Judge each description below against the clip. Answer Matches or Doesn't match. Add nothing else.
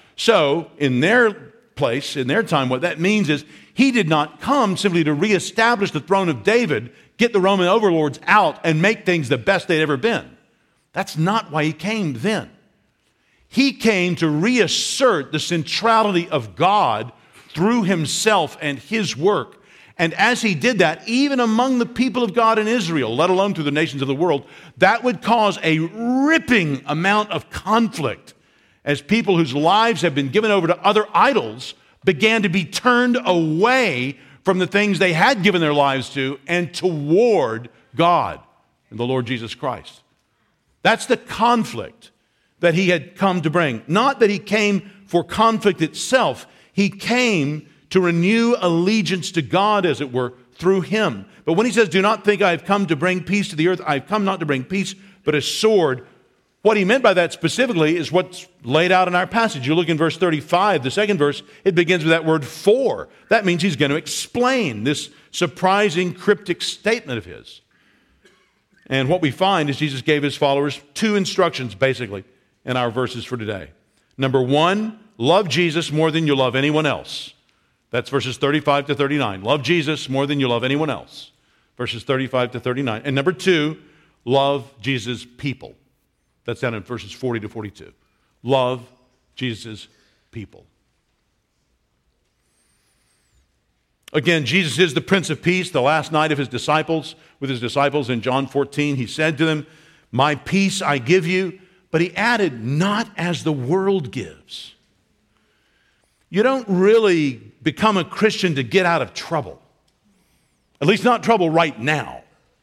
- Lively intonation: Matches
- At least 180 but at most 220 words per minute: Doesn't match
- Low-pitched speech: Doesn't match